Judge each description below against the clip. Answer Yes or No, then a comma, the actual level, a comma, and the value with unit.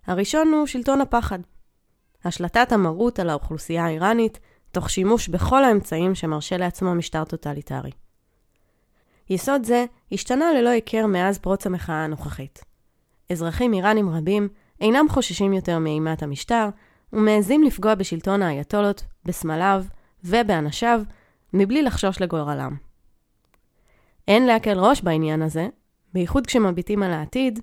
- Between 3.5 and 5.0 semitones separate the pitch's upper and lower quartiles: No, wide, 5.5 semitones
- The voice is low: No, high, 195 Hz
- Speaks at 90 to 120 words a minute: Yes, average, 115 wpm